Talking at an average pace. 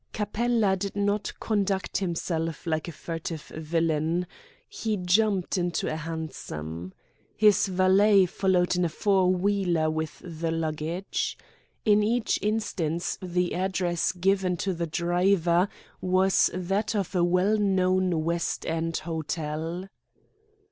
No: slow, 120 wpm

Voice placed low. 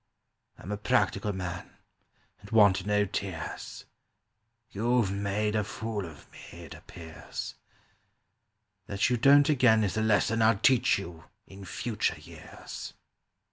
Yes: low, 105 Hz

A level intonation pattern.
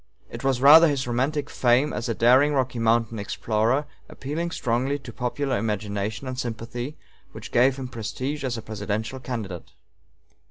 No: average, 3.3 semitones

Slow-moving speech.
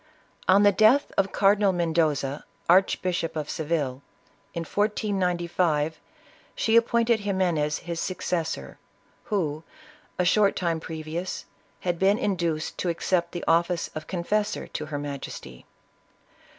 Yes: slow, 120 wpm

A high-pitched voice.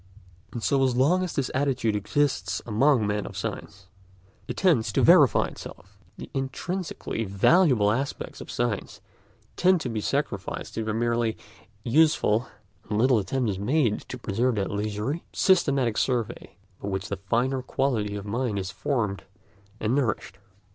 No: low, 120 Hz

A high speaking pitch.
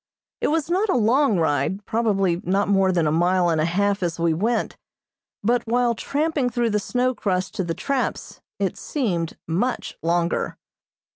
Yes: high, 200 Hz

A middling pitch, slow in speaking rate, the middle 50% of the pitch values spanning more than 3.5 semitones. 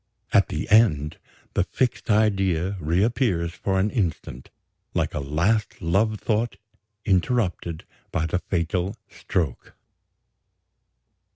No: very low, 95 Hz; slow, 105 wpm; average, 4.4 semitones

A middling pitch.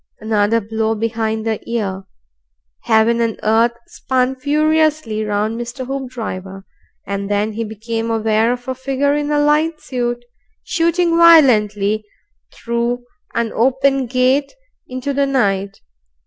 No: high, 235 Hz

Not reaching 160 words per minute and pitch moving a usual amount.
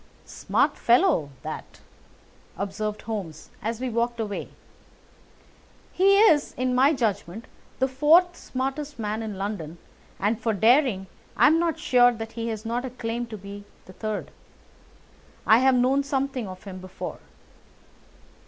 Yes: average, 140 wpm; average, 4.2 semitones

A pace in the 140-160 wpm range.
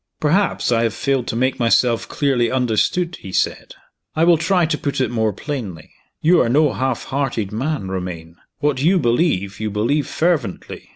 No: average, 175 wpm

